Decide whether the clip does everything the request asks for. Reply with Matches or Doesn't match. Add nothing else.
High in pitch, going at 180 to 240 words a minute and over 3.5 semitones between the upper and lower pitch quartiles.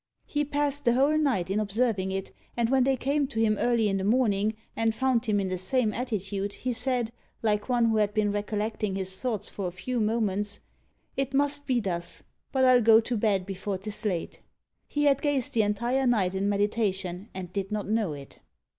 Matches